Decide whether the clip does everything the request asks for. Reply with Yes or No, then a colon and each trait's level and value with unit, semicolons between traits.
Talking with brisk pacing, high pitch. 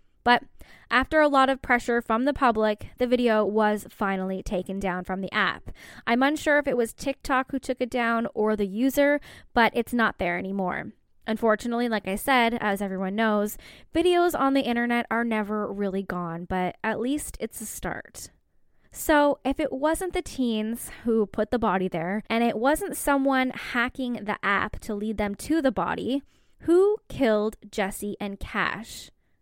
No: average, 175 wpm; high, 230 Hz